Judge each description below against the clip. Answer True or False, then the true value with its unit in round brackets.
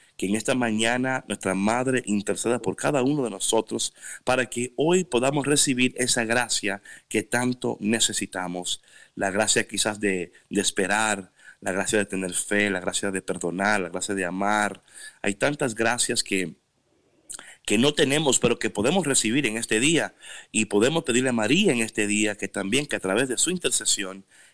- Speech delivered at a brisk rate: False (175 wpm)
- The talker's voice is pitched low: True (110 Hz)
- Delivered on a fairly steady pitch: False (3.9 semitones)